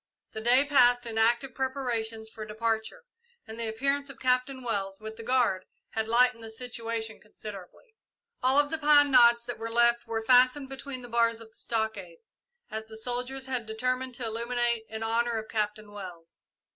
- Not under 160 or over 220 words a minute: Yes, average, 180 wpm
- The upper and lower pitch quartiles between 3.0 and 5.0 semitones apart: No, narrow, 2.5 semitones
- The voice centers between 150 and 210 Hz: No, high, 235 Hz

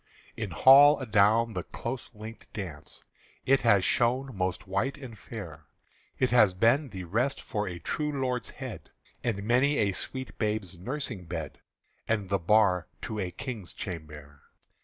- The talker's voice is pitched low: Yes, low, 110 Hz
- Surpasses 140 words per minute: Yes, average, 155 wpm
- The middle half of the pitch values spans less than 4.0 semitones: No, average, 5.3 semitones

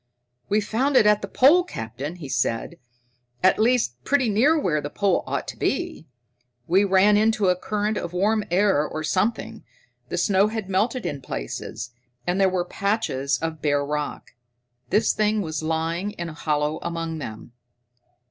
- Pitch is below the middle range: No, medium, 185 Hz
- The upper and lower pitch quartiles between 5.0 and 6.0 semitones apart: Yes, wide, 5.4 semitones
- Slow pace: No, average, 165 wpm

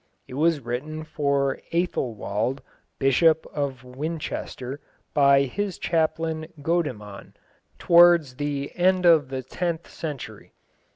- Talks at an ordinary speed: No, slow, 105 wpm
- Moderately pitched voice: Yes, medium, 145 Hz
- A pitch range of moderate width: Yes, average, 3.8 semitones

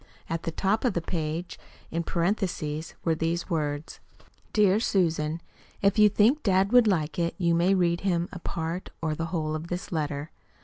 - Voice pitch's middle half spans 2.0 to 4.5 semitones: Yes, average, 3.1 semitones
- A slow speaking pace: No, average, 180 wpm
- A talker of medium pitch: Yes, medium, 170 Hz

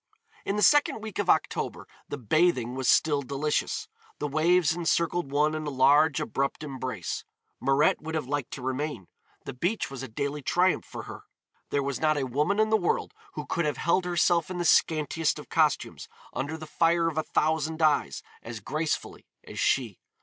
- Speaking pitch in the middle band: Yes, medium, 155 Hz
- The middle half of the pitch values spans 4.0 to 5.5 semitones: No, average, 3.5 semitones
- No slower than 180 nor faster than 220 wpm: Yes, average, 185 wpm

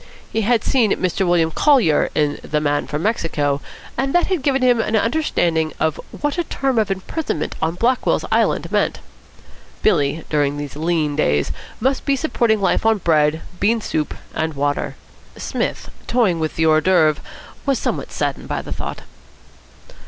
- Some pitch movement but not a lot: No, wide, 7.7 semitones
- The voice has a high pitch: No, medium, 175 Hz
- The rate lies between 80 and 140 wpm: No, average, 165 wpm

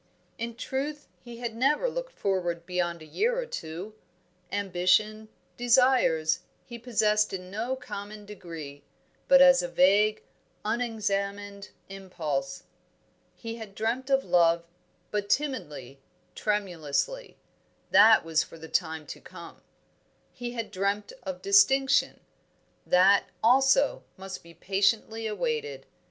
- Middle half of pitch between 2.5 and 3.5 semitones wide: No, average, 5.2 semitones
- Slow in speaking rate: Yes, slow, 120 wpm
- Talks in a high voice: Yes, high, 205 Hz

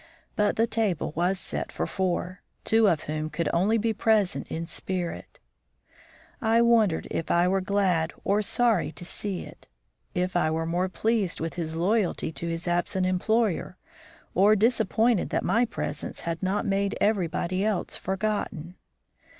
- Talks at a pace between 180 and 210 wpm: No, average, 155 wpm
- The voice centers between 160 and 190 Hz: Yes, medium, 185 Hz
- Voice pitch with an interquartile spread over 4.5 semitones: No, average, 4.0 semitones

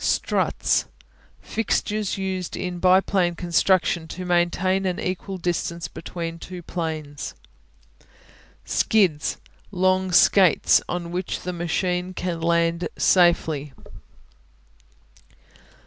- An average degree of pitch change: No, narrow, 1.7 semitones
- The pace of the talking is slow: Yes, slow, 95 wpm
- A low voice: No, medium, 180 Hz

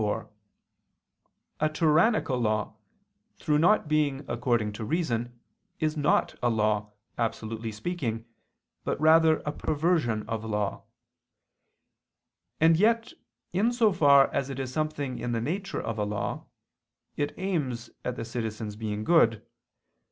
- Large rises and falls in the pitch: Yes, wide, 6.0 semitones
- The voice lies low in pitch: Yes, low, 130 Hz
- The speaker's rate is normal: No, slow, 130 wpm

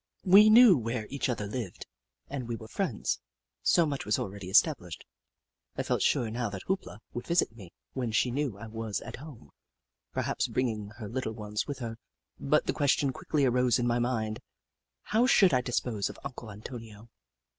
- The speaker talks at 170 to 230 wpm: Yes, average, 195 wpm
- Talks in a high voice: No, low, 120 Hz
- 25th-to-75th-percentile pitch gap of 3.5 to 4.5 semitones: Yes, average, 4.2 semitones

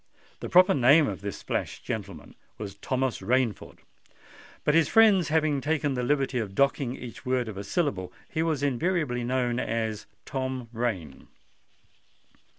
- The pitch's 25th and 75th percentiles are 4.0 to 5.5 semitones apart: Yes, average, 4.8 semitones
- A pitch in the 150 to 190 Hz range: No, low, 130 Hz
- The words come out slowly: No, average, 155 wpm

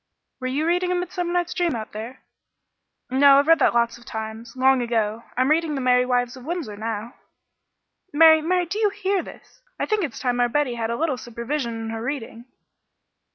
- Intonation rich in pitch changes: Yes, wide, 5.8 semitones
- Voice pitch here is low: No, very high, 260 Hz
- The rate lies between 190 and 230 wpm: Yes, average, 200 wpm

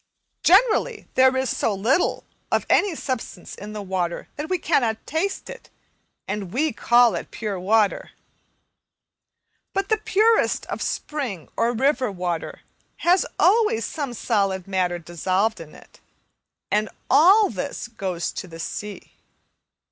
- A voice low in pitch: No, high, 230 Hz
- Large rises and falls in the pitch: Yes, wide, 8.7 semitones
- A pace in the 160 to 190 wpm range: No, slow, 135 wpm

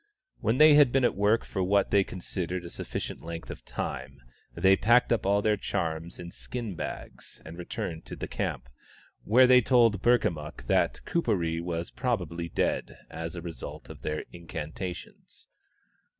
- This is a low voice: Yes, very low, 90 Hz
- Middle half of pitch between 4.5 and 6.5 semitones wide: Yes, wide, 5.5 semitones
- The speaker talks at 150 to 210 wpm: Yes, average, 165 wpm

